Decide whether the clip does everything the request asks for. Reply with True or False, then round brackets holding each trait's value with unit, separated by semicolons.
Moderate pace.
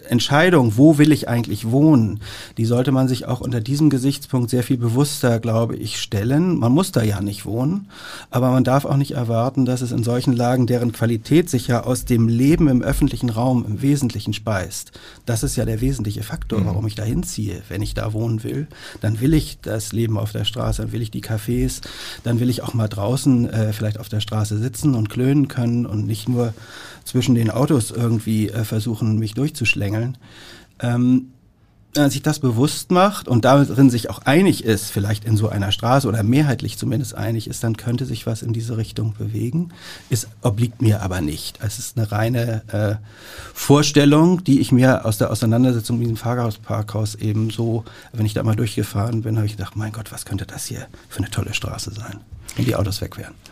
False (205 wpm)